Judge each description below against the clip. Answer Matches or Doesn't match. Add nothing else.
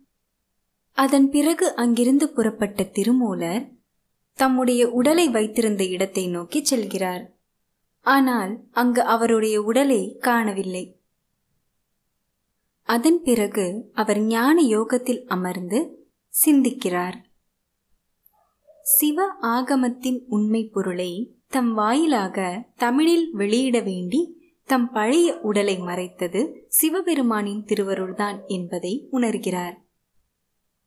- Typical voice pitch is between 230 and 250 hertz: Matches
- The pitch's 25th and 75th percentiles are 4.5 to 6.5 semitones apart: Matches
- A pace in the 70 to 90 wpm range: Matches